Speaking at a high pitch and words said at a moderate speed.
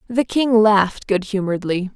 Yes: high, 205 Hz; average, 155 wpm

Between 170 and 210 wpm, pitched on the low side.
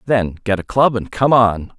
No: fast, 235 wpm; low, 110 Hz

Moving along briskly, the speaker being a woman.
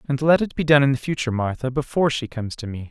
No: fast, 270 wpm; male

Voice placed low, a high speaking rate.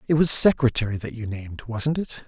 Yes: low, 125 Hz; fast, 210 wpm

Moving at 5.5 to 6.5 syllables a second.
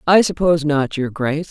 Yes: 5.8 syllables/s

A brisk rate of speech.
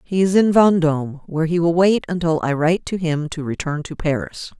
Yes: fast, 220 wpm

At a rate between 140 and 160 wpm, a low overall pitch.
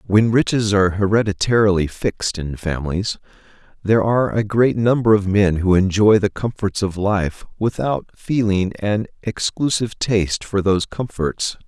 Yes: average, 145 wpm; low, 100 Hz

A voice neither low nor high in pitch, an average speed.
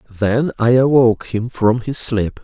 No: low, 115 Hz; average, 170 wpm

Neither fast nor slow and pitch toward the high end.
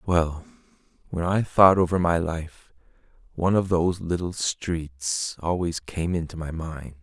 No: average, 145 wpm; very low, 85 Hz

